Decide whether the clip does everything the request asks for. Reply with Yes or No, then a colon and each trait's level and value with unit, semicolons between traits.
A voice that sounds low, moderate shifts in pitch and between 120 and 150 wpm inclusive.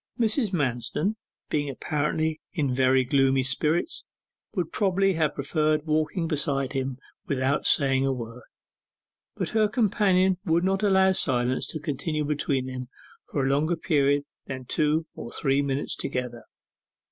No: medium, 150 Hz; average, 4.3 semitones; average, 140 wpm